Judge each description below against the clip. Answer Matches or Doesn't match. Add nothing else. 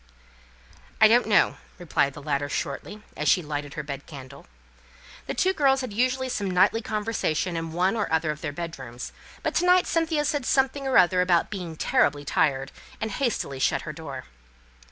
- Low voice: Doesn't match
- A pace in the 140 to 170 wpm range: Doesn't match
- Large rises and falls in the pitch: Matches